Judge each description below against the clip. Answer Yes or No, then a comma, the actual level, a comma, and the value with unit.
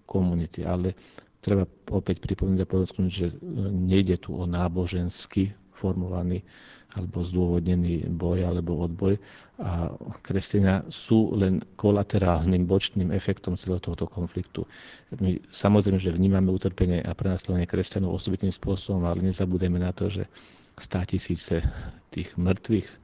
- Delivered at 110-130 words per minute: Yes, average, 120 wpm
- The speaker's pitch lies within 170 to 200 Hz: No, very low, 95 Hz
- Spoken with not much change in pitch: Yes, narrow, 1.6 semitones